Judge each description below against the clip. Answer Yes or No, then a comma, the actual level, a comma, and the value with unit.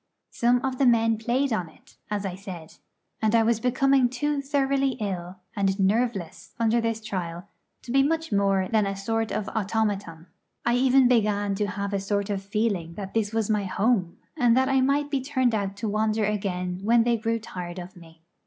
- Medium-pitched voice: No, high, 215 Hz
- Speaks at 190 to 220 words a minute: Yes, average, 200 wpm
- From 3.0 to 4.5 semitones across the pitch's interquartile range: Yes, average, 3.7 semitones